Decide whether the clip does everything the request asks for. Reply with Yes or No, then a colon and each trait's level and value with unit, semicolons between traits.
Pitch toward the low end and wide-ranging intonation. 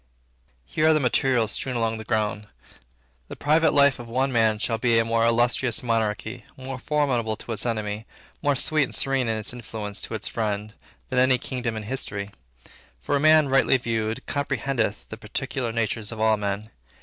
No: low, 115 Hz; average, 3.3 semitones